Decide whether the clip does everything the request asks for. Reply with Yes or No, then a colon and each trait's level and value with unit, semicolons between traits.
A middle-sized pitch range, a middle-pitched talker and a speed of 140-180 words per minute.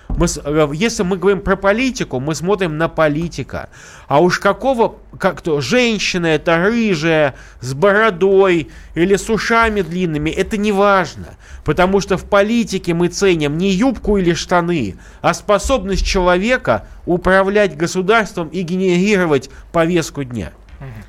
No: average, 4.0 semitones; medium, 180 Hz; average, 130 wpm